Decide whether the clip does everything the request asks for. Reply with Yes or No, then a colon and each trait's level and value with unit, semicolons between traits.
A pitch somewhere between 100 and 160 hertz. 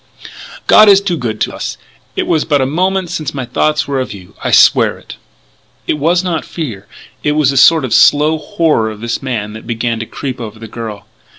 Yes: low, 135 Hz